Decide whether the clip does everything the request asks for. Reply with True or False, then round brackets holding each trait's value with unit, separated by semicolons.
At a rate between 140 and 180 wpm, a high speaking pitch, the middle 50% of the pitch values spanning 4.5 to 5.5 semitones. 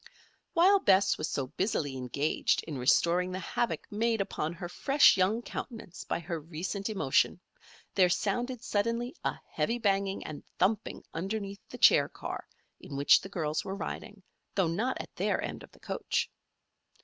True (160 wpm; 195 Hz; 4.8 semitones)